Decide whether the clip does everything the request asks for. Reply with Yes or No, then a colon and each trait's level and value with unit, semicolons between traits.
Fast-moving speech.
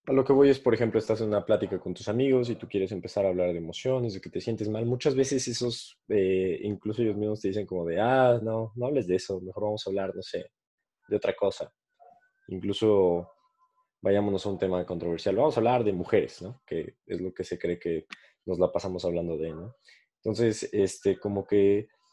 Yes: fast, 220 wpm